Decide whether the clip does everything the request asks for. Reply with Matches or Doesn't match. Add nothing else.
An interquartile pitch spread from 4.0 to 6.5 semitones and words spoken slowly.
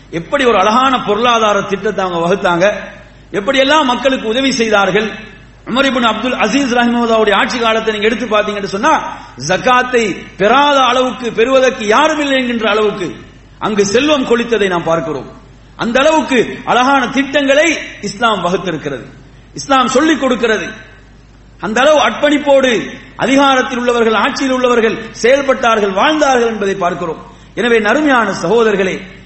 Matches